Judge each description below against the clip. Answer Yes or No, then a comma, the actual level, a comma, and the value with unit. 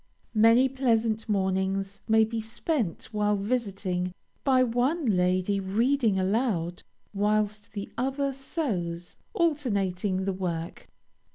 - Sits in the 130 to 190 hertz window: No, high, 210 Hz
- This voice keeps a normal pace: No, slow, 105 wpm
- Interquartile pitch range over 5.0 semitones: No, average, 4.6 semitones